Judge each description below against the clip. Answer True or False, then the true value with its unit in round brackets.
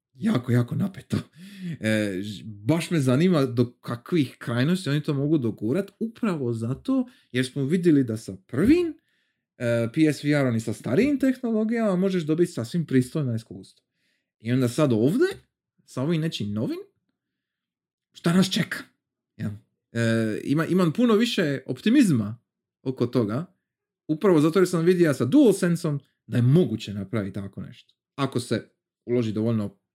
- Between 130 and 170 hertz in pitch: True (140 Hz)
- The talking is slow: False (140 wpm)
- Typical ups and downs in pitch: False (7.6 semitones)